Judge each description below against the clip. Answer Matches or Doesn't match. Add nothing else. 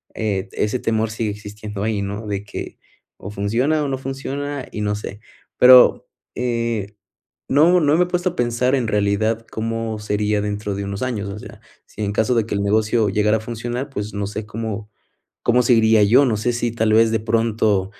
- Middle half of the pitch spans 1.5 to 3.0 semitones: Matches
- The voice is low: Matches